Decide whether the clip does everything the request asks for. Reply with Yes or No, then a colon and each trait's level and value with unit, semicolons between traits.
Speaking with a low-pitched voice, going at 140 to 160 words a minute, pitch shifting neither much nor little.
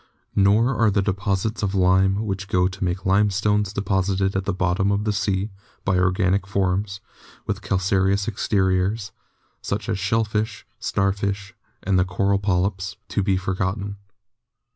No: low, 100 Hz; average, 145 wpm; narrow, 1.3 semitones